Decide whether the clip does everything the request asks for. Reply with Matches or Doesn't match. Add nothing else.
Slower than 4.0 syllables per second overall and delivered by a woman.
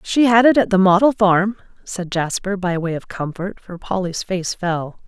Doesn't match